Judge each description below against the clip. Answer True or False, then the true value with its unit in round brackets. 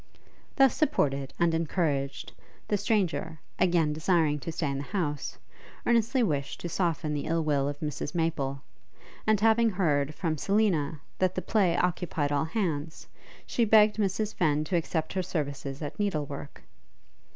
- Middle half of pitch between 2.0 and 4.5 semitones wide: False (5.0 semitones)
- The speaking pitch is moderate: True (165 Hz)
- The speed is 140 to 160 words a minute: True (155 wpm)